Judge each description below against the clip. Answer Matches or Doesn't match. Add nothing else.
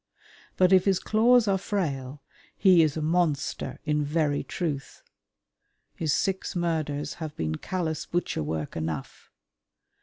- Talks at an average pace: Doesn't match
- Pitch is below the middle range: Doesn't match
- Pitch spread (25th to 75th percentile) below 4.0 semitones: Doesn't match